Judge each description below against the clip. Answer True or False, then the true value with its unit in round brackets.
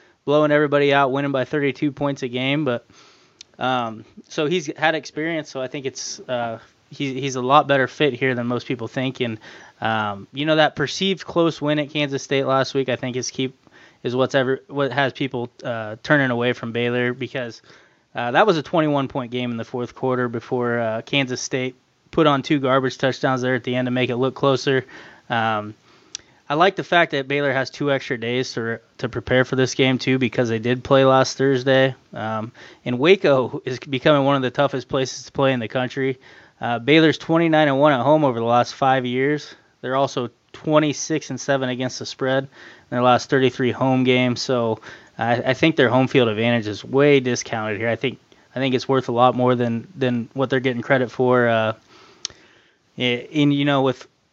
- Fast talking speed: True (210 wpm)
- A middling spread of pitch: False (2.3 semitones)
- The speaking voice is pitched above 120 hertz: True (130 Hz)